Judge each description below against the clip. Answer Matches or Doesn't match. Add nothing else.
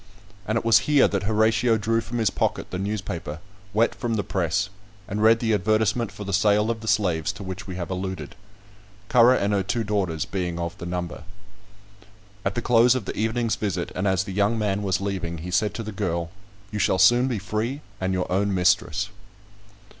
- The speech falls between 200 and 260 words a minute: Matches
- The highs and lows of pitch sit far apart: Doesn't match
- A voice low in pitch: Matches